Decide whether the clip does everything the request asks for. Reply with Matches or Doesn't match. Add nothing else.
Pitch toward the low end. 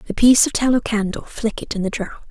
Doesn't match